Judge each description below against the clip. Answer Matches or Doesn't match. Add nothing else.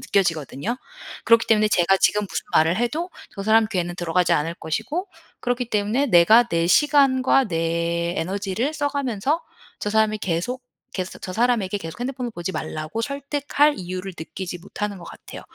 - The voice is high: Matches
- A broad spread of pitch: Matches